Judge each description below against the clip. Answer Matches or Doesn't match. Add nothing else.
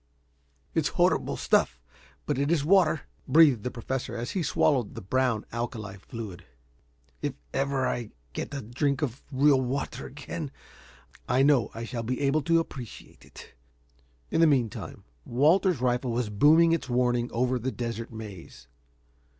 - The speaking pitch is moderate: Doesn't match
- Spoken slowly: Doesn't match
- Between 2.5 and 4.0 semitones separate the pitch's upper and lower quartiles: Matches